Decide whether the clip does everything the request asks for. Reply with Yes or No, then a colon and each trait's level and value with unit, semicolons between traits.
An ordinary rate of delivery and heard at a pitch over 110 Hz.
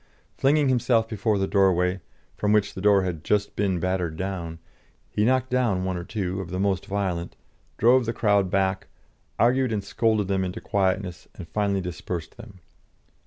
No: average, 170 wpm; low, 100 Hz